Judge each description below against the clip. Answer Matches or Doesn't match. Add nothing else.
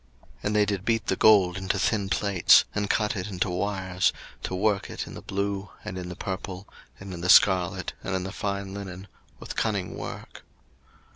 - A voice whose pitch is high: Doesn't match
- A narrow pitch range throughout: Matches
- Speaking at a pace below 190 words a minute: Doesn't match